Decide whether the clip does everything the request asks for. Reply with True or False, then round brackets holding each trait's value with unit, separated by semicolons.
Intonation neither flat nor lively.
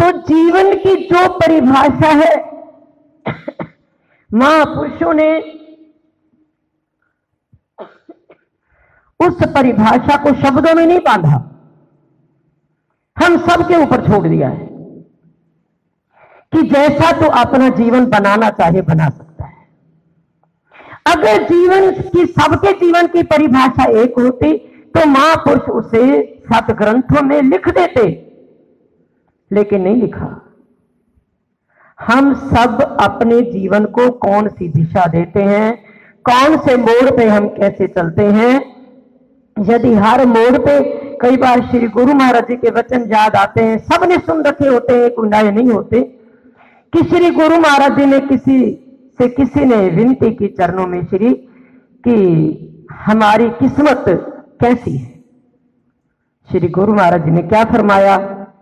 False (5.9 semitones)